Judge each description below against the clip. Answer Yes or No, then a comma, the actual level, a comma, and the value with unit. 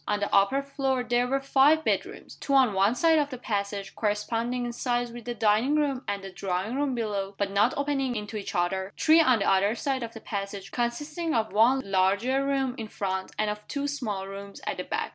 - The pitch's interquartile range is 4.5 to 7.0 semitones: Yes, average, 5.0 semitones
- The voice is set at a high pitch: Yes, high, 235 Hz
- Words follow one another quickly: Yes, fast, 220 wpm